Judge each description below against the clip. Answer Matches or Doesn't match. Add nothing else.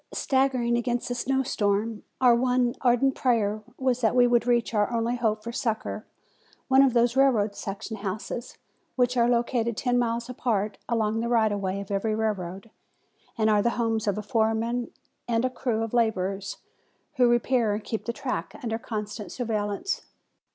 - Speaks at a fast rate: Doesn't match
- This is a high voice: Matches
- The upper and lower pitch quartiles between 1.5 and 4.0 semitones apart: Matches